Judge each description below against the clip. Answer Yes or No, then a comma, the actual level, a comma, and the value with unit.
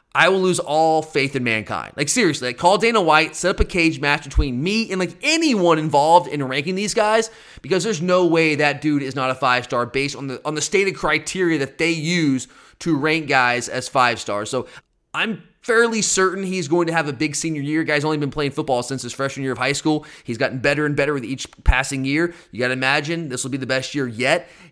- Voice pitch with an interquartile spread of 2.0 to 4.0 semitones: No, average, 4.5 semitones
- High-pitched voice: No, medium, 155 Hz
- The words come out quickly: Yes, fast, 240 wpm